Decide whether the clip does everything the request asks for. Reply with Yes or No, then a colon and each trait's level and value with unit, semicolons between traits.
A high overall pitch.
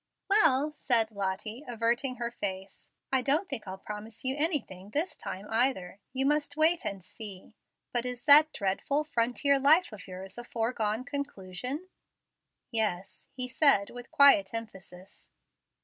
Yes: high, 240 Hz